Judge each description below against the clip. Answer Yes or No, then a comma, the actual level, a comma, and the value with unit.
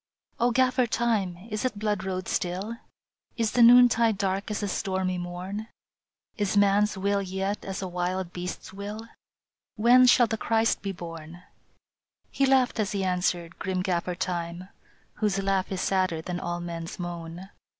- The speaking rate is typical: Yes, average, 170 wpm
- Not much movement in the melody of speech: No, average, 3.2 semitones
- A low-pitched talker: No, high, 195 Hz